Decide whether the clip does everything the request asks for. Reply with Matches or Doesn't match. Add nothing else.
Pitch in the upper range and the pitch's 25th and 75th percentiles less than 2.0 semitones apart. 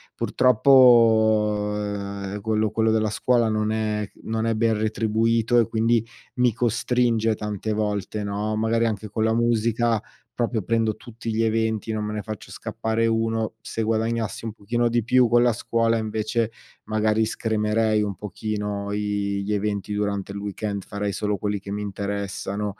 Doesn't match